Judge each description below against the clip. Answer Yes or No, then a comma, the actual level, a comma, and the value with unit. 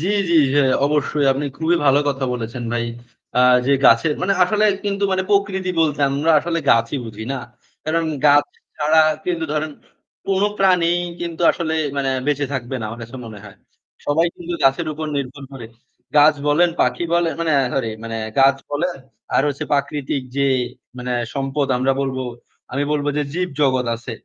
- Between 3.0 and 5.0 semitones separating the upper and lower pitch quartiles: Yes, average, 3.8 semitones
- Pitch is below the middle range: No, medium, 145 Hz